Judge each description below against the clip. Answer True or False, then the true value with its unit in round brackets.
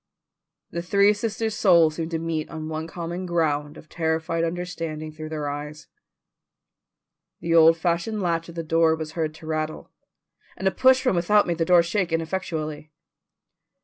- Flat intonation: True (2.0 semitones)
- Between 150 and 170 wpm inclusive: True (165 wpm)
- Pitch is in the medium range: True (165 Hz)